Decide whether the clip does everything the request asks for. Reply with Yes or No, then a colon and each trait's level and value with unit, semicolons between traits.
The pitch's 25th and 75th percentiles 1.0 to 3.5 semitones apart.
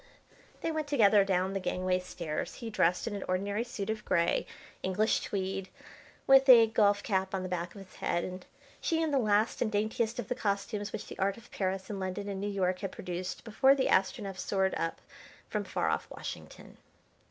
Yes: average, 2.8 semitones